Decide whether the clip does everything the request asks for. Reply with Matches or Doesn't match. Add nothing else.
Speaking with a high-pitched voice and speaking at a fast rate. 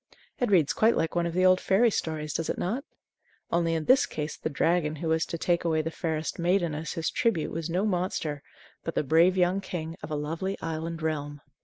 Doesn't match